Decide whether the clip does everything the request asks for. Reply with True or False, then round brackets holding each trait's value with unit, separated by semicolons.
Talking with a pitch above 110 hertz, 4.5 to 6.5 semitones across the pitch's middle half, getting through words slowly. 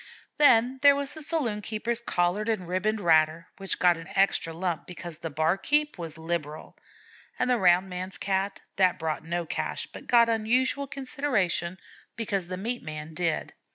False (190 Hz; 5.4 semitones; 165 wpm)